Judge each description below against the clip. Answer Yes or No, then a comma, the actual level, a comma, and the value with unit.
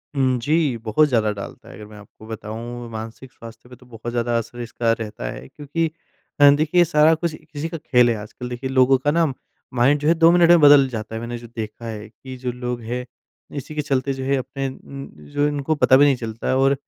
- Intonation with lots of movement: No, average, 3.8 semitones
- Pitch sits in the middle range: No, low, 125 Hz